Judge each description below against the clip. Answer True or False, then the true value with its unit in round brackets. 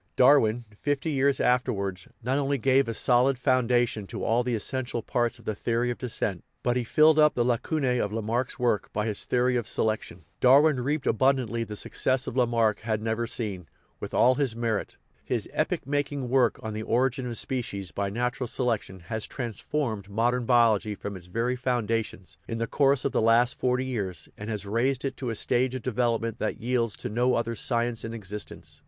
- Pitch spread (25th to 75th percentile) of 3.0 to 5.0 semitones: False (2.6 semitones)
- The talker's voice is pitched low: True (120 Hz)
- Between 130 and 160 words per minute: False (200 wpm)